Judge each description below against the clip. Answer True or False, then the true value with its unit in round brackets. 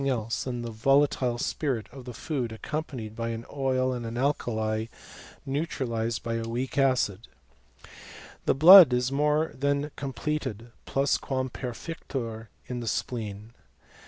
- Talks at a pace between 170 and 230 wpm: False (145 wpm)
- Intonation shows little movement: False (3.2 semitones)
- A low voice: True (125 Hz)